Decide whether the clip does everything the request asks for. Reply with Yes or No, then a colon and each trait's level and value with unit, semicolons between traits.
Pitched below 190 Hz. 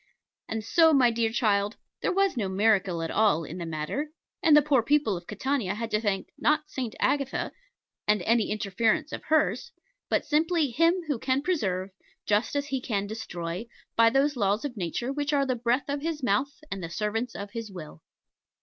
No: high, 230 Hz